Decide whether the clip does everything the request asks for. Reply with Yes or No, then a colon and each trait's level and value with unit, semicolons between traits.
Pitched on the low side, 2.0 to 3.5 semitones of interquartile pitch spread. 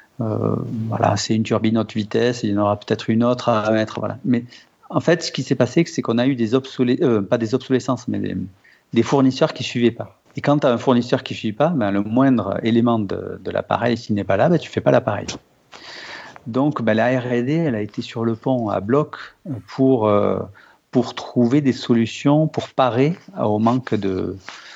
Yes: low, 120 Hz; average, 3.0 semitones